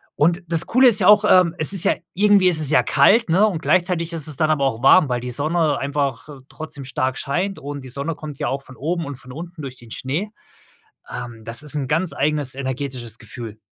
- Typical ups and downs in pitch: Yes, average, 4.6 semitones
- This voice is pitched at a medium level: Yes, medium, 150 Hz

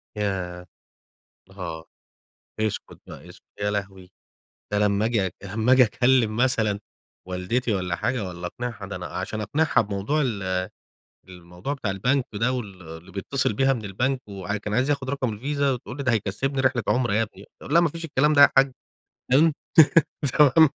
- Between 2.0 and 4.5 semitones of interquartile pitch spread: No, average, 5.2 semitones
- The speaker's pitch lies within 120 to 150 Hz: No, low, 110 Hz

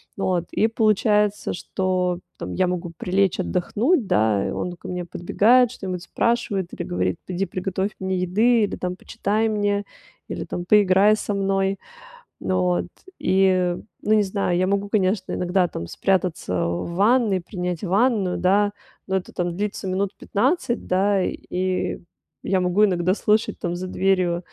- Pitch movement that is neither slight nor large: No, narrow, 2.3 semitones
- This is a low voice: No, high, 190 Hz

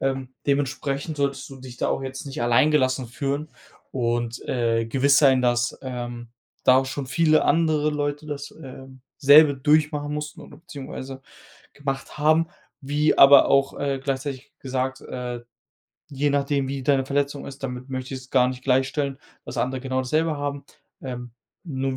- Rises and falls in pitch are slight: Yes, narrow, 1.9 semitones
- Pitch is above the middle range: No, low, 135 Hz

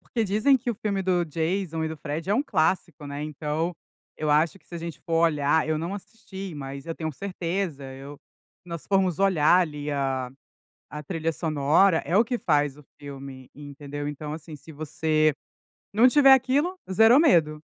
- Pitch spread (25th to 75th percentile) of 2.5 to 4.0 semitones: No, average, 4.6 semitones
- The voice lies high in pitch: No, medium, 160 Hz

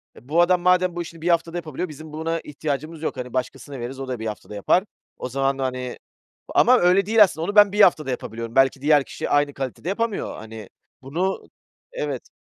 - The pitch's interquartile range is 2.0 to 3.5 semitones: No, average, 5.2 semitones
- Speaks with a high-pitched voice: No, medium, 150 Hz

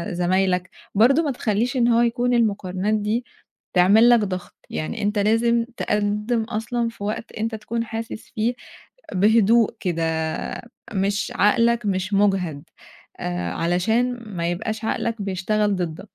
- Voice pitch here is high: Yes, high, 210 Hz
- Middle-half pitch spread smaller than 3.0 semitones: No, average, 3.7 semitones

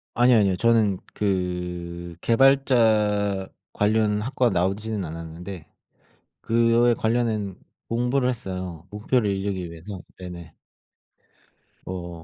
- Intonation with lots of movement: No, average, 4.5 semitones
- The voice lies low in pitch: Yes, low, 100 Hz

